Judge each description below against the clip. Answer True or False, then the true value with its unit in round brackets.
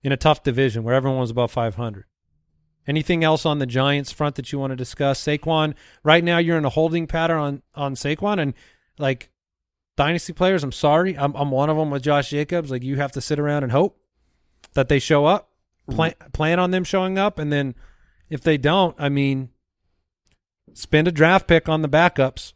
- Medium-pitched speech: True (145 Hz)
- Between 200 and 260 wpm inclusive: True (205 wpm)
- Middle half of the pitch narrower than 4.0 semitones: True (3.3 semitones)